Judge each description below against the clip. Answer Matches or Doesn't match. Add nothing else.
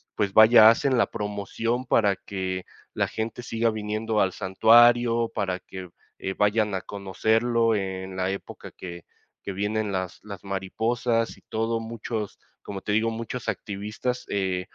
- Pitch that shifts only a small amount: Doesn't match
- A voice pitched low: Matches